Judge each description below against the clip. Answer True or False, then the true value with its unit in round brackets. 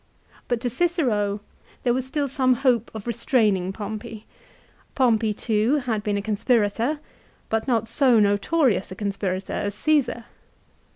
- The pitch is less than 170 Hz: False (225 Hz)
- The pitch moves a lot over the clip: False (3.8 semitones)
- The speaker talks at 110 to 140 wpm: True (135 wpm)